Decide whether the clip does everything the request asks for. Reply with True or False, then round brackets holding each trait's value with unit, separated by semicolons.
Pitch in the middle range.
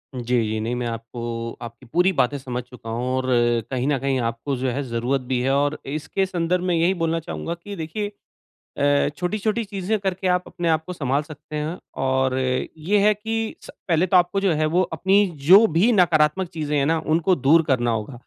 True (155 Hz)